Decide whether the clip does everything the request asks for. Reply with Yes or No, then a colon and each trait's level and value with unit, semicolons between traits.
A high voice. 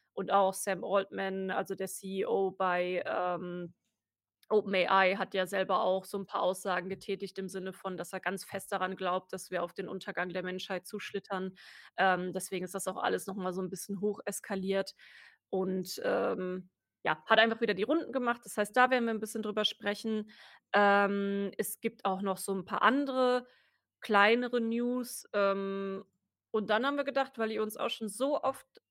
Yes: high, 195 Hz